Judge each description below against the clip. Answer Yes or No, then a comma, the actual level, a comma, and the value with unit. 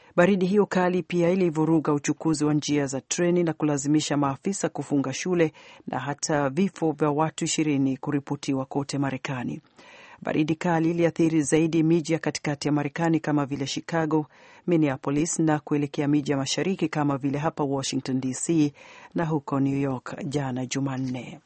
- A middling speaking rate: No, fast, 150 wpm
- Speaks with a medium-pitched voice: Yes, medium, 150 Hz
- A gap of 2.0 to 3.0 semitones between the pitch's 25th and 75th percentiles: Yes, narrow, 2.6 semitones